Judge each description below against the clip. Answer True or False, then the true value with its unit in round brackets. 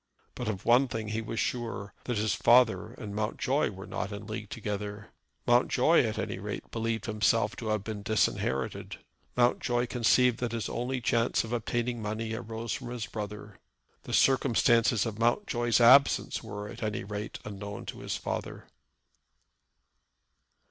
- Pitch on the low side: True (115 Hz)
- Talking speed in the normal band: True (155 wpm)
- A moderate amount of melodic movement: False (2.3 semitones)